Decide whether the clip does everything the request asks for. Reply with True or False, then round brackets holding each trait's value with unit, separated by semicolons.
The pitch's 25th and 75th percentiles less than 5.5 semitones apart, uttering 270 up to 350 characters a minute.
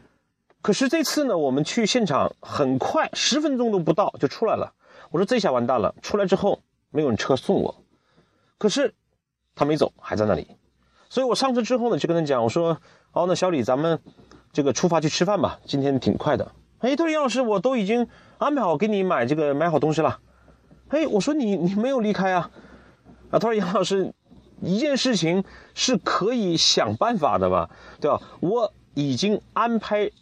False (7.3 semitones; 280 characters per minute)